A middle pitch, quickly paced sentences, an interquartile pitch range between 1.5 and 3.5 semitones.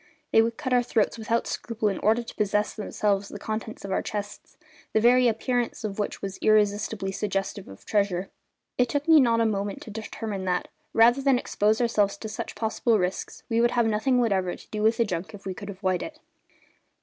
No: high, 215 Hz; fast, 210 wpm; narrow, 2.6 semitones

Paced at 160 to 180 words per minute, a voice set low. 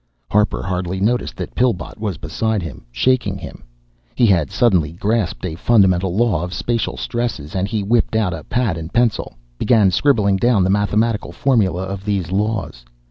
Yes: average, 170 wpm; low, 100 Hz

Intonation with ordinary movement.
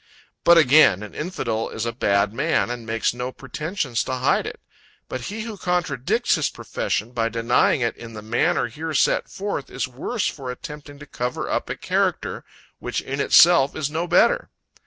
No: wide, 5.7 semitones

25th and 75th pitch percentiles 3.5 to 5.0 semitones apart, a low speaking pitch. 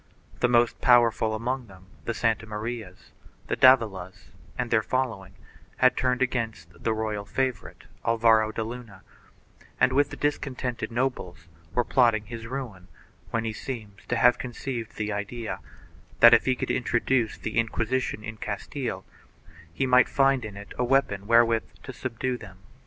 No: average, 2.7 semitones; low, 115 Hz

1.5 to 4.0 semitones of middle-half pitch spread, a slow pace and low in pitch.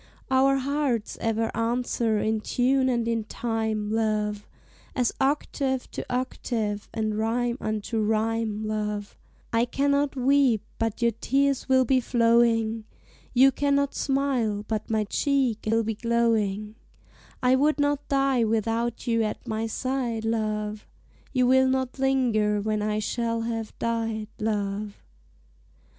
No: average, 3.2 semitones; slow, 130 wpm; high, 230 Hz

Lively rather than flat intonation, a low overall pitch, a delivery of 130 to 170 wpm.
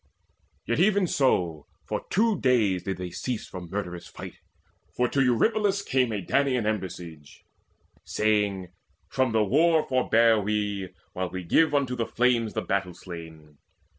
Yes: wide, 6.0 semitones; low, 110 Hz; average, 145 wpm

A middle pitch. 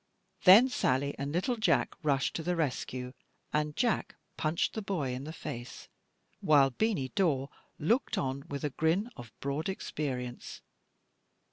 Yes: medium, 150 Hz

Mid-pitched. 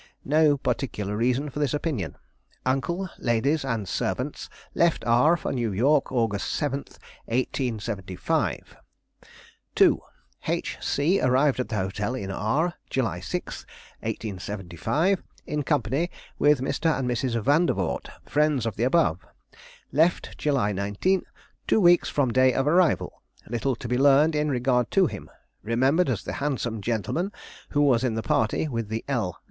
No: low, 130 Hz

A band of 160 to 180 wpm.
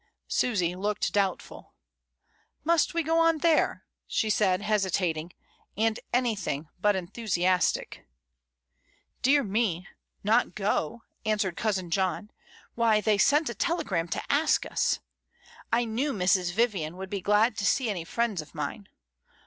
No: slow, 135 wpm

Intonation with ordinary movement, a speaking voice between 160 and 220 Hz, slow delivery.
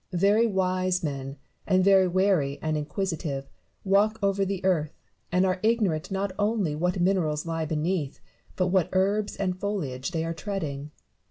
No: average, 3.9 semitones; medium, 185 Hz; average, 155 wpm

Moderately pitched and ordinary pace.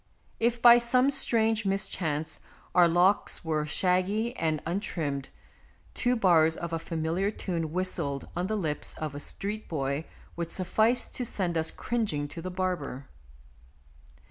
Yes: medium, 180 Hz; average, 150 wpm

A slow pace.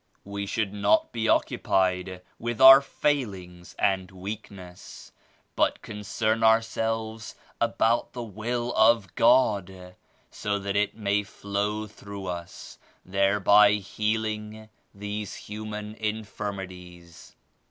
Yes: slow, 105 wpm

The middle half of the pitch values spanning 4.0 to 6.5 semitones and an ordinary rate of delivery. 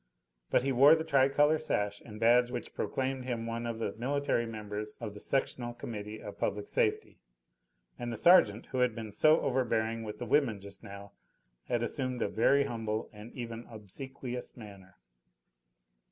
No: average, 3.5 semitones; average, 170 wpm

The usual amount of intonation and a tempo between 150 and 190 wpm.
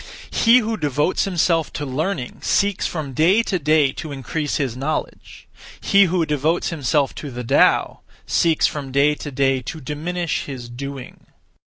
Yes: average, 3.8 semitones; average, 160 wpm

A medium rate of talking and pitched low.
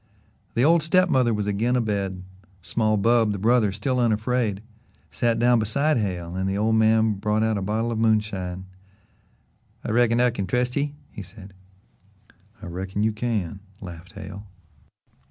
Yes: average, 170 wpm; low, 110 Hz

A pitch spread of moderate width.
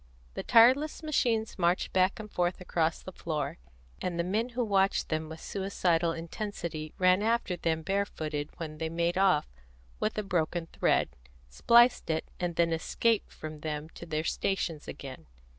Yes: average, 4.0 semitones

